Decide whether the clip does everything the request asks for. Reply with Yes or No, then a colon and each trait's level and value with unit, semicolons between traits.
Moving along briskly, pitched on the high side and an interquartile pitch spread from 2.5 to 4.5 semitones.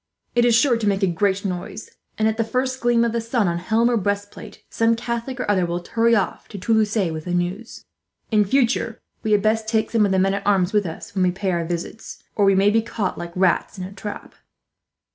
Yes: fast, 245 wpm; high, 205 Hz; average, 3.3 semitones